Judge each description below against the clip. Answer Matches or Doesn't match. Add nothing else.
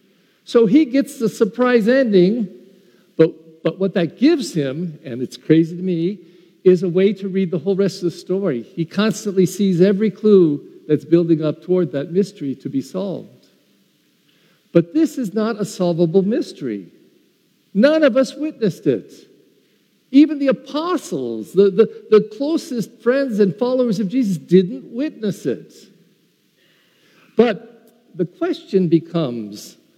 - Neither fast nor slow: Matches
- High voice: Matches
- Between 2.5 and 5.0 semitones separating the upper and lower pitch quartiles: Doesn't match